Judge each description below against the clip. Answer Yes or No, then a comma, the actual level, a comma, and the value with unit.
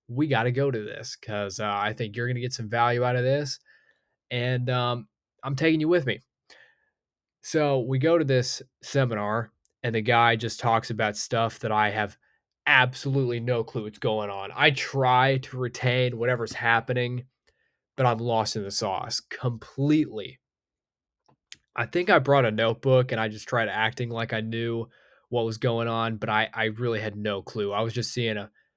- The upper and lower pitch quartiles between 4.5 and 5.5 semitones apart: No, average, 2.7 semitones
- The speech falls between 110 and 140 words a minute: No, average, 190 wpm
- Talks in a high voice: No, low, 120 Hz